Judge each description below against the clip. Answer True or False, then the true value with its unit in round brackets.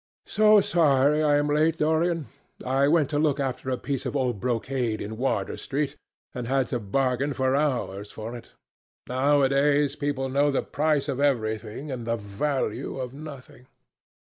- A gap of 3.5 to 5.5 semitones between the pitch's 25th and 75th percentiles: False (2.8 semitones)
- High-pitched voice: False (135 Hz)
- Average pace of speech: True (165 wpm)